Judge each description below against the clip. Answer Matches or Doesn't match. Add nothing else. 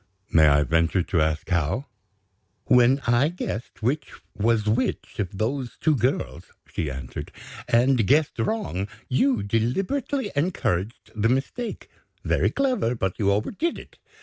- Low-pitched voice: Matches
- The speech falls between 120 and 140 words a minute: Matches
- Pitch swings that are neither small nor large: Doesn't match